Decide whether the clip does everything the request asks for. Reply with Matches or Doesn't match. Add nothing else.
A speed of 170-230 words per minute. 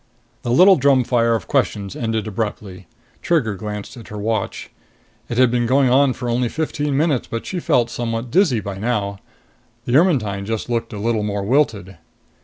Matches